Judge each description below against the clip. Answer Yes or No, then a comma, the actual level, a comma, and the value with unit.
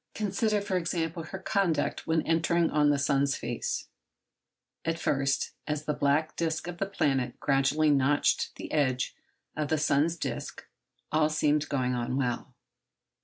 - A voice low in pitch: No, medium, 150 Hz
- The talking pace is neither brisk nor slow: Yes, average, 150 wpm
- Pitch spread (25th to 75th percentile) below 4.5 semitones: Yes, average, 3.0 semitones